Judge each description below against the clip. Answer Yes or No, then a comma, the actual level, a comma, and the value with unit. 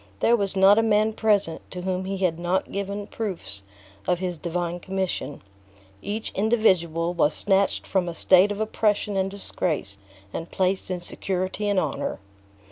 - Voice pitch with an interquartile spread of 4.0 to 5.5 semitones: No, average, 2.7 semitones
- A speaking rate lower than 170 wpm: Yes, average, 160 wpm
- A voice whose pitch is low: No, high, 190 Hz